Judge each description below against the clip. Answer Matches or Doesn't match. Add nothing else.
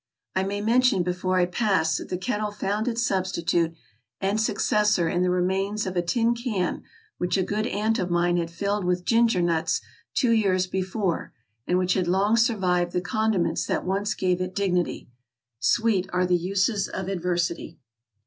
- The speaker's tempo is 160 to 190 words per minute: Matches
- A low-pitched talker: Doesn't match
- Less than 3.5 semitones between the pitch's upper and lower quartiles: Matches